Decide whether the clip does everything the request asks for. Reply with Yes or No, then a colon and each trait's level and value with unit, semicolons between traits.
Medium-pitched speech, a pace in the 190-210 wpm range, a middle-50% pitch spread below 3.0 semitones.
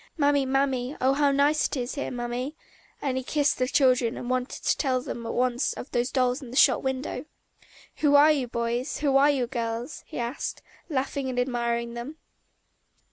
No: very high, 255 Hz; average, 195 wpm; narrow, 2.5 semitones